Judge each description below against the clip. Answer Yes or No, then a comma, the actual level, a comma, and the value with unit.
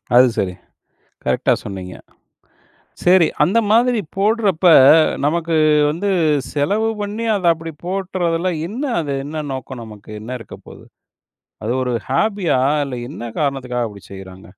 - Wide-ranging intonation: Yes, wide, 7.6 semitones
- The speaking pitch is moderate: Yes, medium, 160 Hz